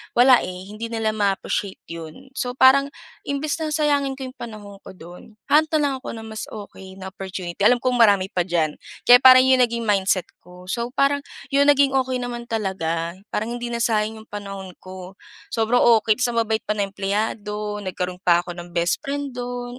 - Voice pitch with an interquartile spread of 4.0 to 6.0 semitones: Yes, average, 4.8 semitones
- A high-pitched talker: Yes, high, 220 Hz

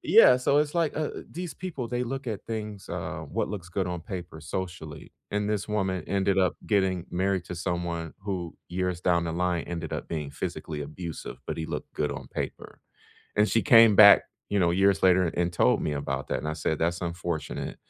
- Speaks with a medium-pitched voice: No, very low, 90 Hz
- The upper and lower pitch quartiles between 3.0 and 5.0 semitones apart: Yes, average, 3.7 semitones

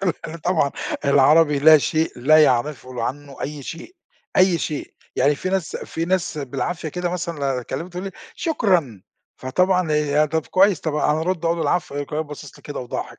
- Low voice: No, medium, 155 Hz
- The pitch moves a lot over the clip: No, average, 3.6 semitones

